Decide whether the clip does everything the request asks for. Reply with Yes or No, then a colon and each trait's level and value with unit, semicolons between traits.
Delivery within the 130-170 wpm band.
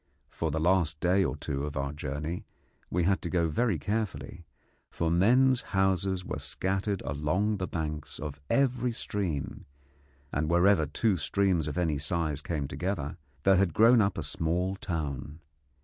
Yes: average, 160 wpm